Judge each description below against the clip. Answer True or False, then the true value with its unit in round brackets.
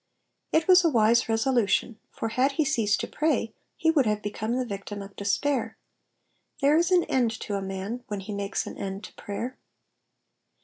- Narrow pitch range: False (5.2 semitones)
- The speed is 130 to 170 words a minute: False (190 wpm)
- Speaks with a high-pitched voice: True (230 Hz)